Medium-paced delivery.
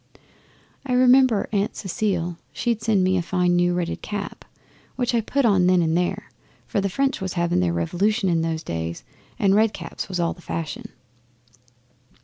Yes: average, 180 wpm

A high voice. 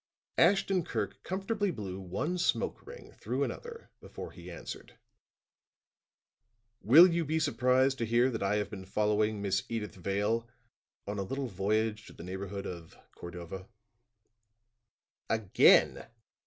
No: low, 110 Hz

